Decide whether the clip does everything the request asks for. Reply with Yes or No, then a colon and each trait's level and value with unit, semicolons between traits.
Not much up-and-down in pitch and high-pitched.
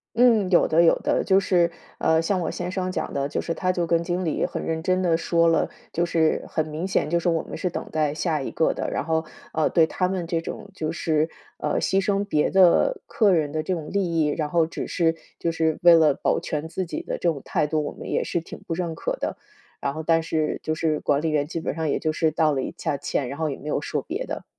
No: narrow, 2.1 semitones; medium, 165 Hz